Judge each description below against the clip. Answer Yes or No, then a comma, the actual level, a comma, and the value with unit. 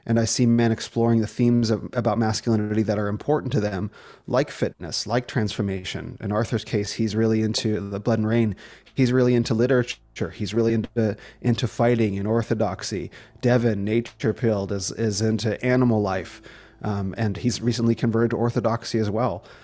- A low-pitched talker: Yes, low, 115 Hz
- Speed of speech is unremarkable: Yes, average, 175 wpm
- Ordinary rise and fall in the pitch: No, narrow, 1.9 semitones